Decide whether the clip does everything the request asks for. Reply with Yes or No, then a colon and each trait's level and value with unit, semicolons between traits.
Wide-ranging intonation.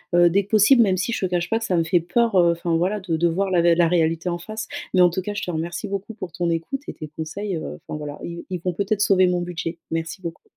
No: average, 2.9 semitones